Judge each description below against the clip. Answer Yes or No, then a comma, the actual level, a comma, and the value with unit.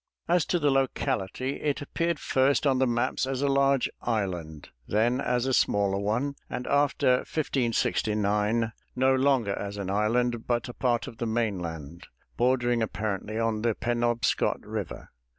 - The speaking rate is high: No, average, 150 wpm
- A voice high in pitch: No, low, 120 Hz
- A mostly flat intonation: No, average, 3.9 semitones